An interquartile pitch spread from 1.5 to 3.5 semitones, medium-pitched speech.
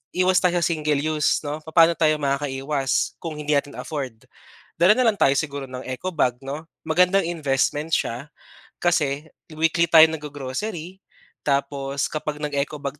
Yes: average, 2.9 semitones; medium, 150 Hz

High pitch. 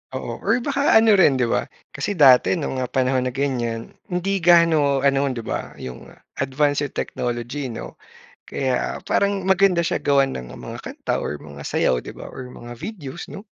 No: medium, 140 Hz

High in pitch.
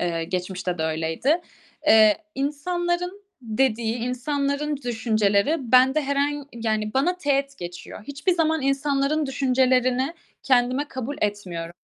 Yes: very high, 260 Hz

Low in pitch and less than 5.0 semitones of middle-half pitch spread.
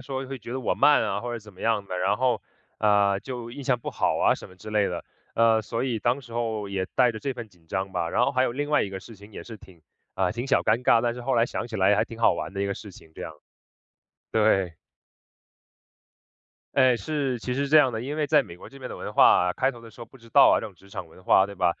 Yes: low, 115 Hz; average, 4.3 semitones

